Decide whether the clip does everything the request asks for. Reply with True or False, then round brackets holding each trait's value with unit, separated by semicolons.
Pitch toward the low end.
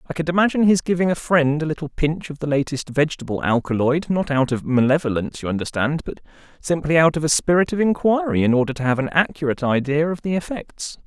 False (150 Hz)